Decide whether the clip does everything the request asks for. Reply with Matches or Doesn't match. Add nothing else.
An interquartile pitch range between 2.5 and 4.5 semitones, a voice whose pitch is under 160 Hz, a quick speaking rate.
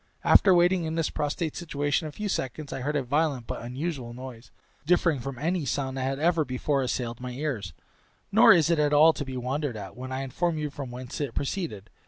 Matches